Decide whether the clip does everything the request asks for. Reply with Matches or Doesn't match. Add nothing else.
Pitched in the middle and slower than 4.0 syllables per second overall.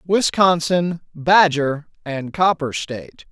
Matches